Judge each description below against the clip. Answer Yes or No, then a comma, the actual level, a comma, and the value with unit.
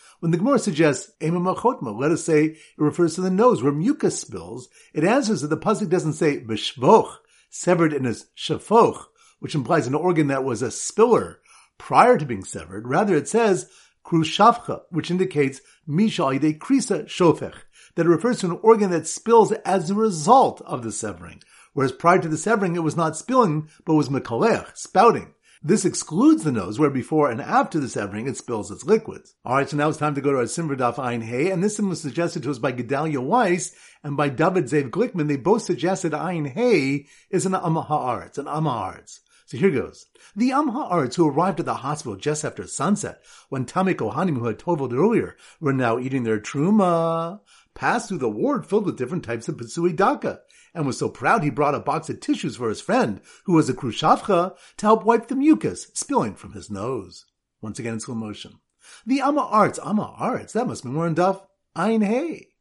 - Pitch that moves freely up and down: Yes, wide, 6.1 semitones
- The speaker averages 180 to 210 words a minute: Yes, average, 195 wpm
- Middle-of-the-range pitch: Yes, medium, 170 Hz